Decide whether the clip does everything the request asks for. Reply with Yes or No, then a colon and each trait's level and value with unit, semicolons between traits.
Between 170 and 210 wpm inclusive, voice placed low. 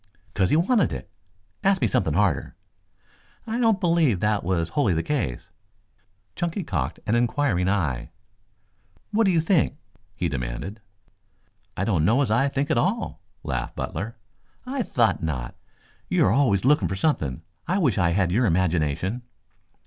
No: average, 155 wpm; low, 110 Hz